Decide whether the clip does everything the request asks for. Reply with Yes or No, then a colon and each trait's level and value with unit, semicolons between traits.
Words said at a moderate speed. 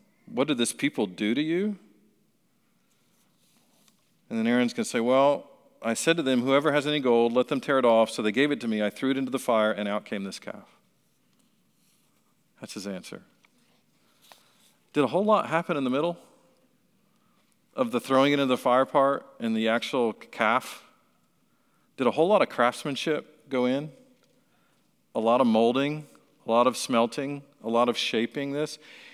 Yes: average, 180 wpm